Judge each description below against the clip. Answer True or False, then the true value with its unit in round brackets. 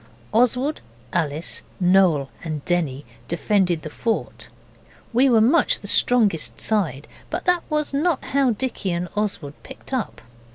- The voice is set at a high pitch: True (205 Hz)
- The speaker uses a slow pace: True (130 wpm)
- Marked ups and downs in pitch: True (7.5 semitones)